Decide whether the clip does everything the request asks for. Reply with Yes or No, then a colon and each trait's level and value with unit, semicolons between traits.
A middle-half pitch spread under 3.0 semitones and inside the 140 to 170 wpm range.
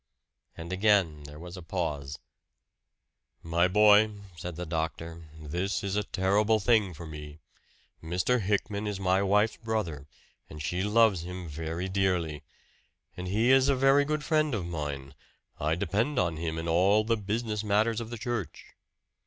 No: average, 4.7 semitones; average, 160 wpm